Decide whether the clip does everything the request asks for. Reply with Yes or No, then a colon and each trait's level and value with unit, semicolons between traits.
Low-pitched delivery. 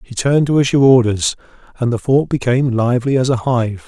Yes: low, 125 Hz